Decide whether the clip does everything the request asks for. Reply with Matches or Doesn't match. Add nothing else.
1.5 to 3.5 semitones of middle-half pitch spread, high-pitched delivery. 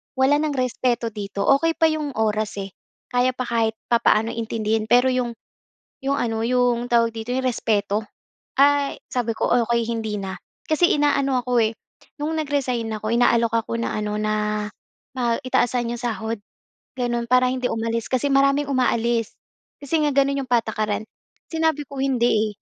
Matches